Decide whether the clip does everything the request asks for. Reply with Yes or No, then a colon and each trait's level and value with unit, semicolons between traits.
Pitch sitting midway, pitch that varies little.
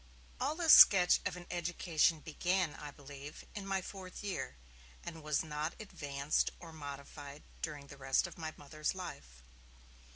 No: medium, 155 Hz; average, 4.0 semitones